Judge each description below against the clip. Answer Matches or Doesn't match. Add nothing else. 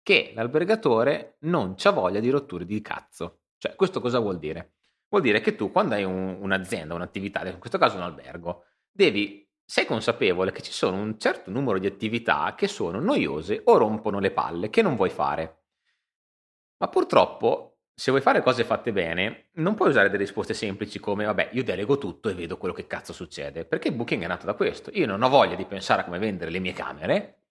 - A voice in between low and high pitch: Doesn't match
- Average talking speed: Doesn't match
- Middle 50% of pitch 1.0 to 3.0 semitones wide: Doesn't match